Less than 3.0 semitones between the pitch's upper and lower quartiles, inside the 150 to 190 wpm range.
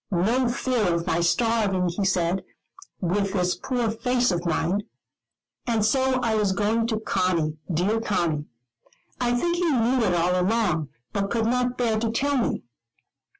No: average, 5.0 semitones; average, 165 wpm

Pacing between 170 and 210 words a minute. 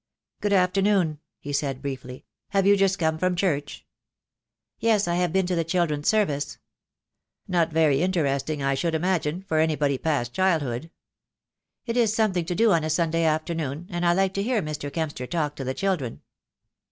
Yes: average, 175 wpm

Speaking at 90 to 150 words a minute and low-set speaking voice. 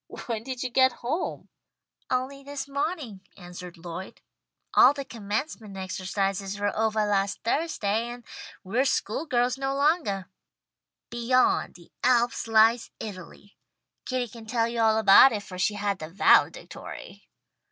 No: average, 140 wpm; high, 225 Hz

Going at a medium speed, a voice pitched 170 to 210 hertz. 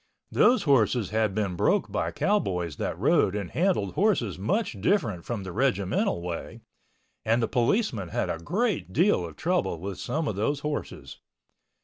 No: average, 160 wpm; low, 110 Hz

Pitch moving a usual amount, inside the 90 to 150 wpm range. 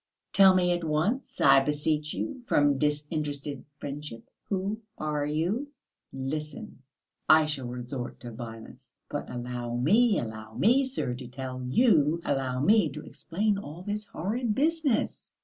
No: wide, 7.1 semitones; average, 140 wpm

